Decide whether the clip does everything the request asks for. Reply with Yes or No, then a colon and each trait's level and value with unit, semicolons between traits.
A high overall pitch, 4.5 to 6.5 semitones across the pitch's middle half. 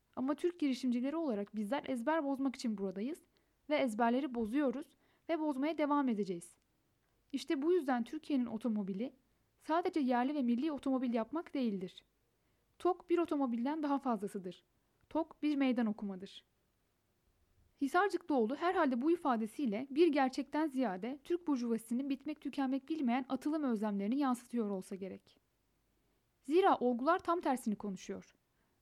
Yes: very high, 265 Hz; average, 4.9 semitones